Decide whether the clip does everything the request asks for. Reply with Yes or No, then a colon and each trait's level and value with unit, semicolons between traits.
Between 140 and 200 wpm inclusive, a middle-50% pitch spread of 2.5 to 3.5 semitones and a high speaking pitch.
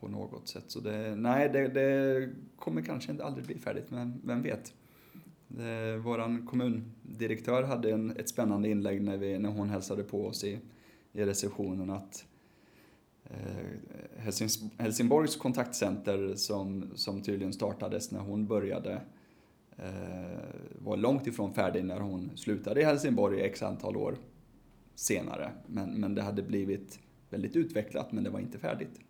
No: average, 150 wpm; average, 3.2 semitones; low, 105 Hz